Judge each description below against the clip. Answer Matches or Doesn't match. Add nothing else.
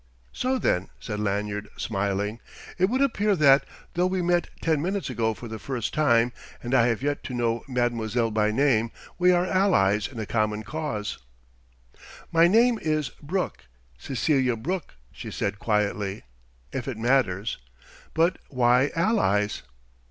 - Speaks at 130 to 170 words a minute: Matches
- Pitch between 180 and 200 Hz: Doesn't match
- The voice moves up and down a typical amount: Doesn't match